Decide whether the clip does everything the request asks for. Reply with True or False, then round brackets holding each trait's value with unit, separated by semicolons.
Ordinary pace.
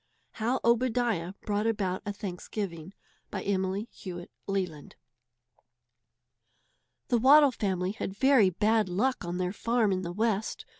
False (130 wpm)